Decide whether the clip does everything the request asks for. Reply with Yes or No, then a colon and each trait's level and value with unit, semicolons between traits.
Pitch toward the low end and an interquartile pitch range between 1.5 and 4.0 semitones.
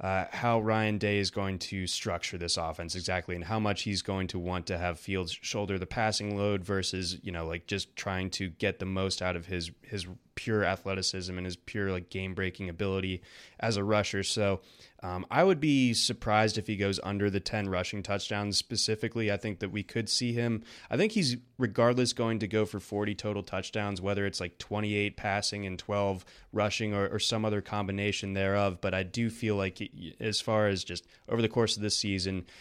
Yes: low, 100 Hz; narrow, 2.4 semitones